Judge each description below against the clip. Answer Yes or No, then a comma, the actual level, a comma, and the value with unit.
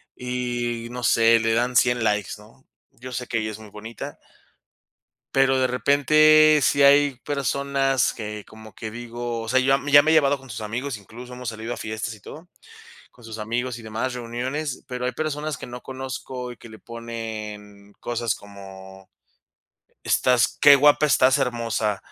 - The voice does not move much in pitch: No, average, 3.3 semitones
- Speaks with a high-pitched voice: No, low, 120 Hz